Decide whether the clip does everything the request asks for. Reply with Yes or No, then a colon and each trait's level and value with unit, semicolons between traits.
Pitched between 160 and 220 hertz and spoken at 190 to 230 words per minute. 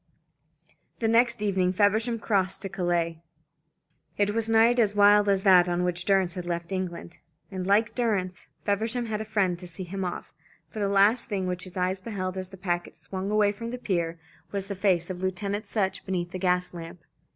Yes: high, 190 Hz; average, 200 wpm